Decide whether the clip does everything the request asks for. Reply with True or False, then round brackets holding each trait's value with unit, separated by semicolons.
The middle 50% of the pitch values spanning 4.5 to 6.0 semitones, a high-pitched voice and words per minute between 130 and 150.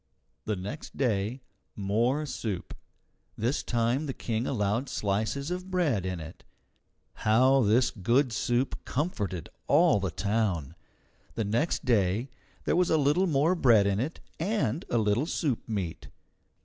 False (5.4 semitones; 120 Hz; 140 wpm)